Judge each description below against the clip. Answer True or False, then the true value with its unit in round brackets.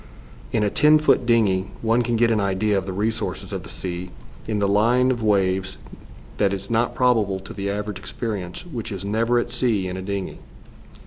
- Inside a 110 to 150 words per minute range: False (200 wpm)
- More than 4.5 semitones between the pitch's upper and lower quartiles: False (3.1 semitones)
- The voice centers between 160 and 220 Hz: False (105 Hz)